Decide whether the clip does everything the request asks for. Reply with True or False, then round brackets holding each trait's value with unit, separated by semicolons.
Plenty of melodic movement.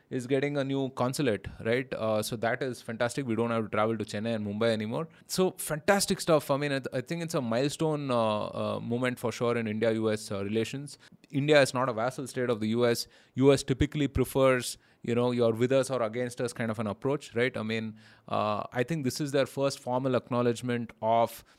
False (3.3 semitones)